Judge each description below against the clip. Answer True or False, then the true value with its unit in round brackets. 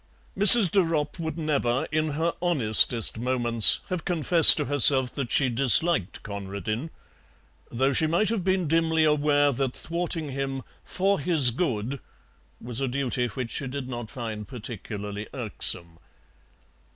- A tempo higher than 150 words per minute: False (140 wpm)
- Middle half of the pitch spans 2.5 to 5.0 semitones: False (5.4 semitones)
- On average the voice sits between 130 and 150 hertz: True (135 Hz)